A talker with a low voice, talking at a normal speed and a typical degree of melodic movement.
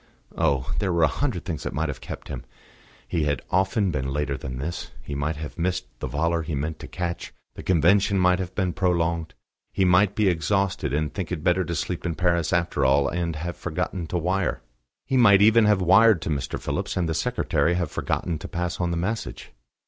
No: very low, 85 Hz; fast, 215 wpm; average, 3.2 semitones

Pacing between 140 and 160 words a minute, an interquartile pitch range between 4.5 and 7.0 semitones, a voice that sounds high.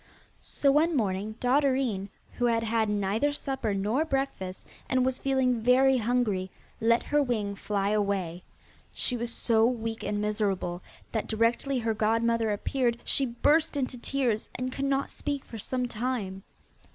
No: average, 150 wpm; average, 3.9 semitones; high, 235 Hz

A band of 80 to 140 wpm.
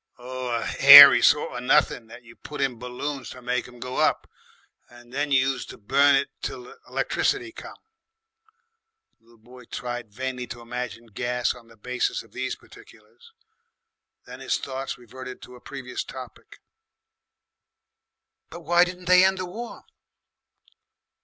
No: average, 155 wpm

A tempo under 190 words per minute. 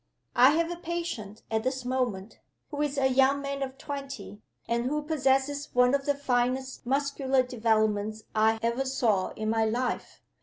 Yes: average, 165 wpm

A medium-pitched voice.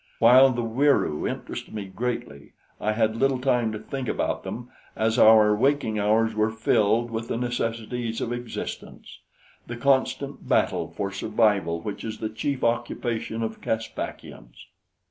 No: low, 115 Hz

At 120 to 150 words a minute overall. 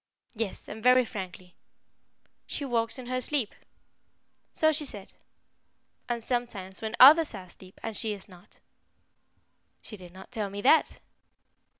Yes: average, 140 wpm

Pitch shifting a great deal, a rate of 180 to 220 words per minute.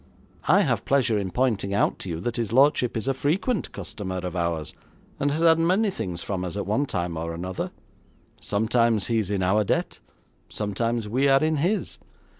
Yes: wide, 6.5 semitones; average, 195 wpm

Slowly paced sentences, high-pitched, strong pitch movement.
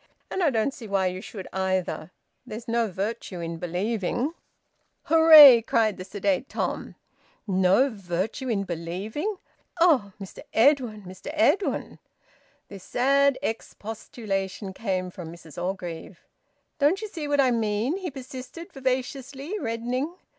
Yes: slow, 130 wpm; high, 225 Hz; wide, 6.5 semitones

